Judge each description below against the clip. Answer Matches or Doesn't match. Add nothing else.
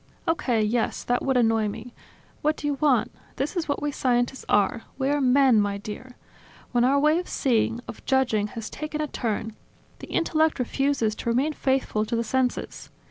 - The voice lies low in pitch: Doesn't match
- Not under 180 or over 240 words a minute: Matches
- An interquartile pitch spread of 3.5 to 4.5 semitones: Matches